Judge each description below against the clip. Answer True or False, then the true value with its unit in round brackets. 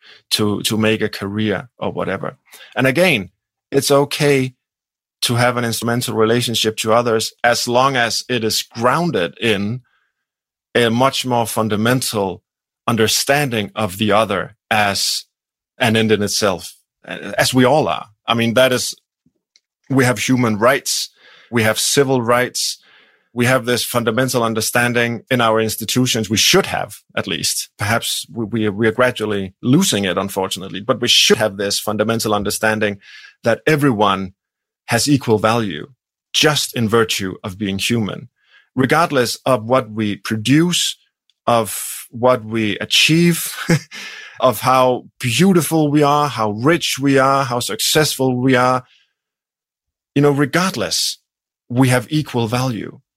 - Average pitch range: True (3.3 semitones)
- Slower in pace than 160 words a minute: True (140 wpm)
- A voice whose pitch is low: True (120 Hz)